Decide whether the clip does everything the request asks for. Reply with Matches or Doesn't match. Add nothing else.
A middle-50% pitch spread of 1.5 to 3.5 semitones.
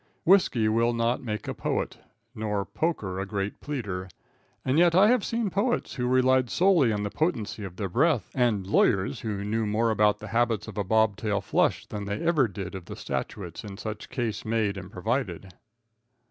Doesn't match